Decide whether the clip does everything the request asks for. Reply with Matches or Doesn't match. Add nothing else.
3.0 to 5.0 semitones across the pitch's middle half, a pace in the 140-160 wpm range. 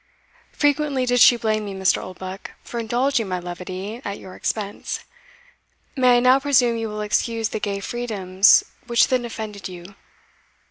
Matches